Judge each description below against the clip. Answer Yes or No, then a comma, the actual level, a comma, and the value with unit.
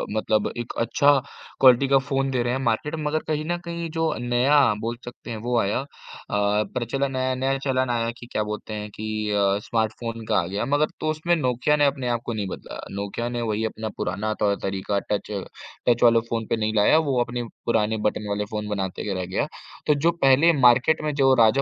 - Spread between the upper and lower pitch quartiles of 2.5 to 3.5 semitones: No, average, 4.2 semitones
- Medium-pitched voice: No, low, 120 Hz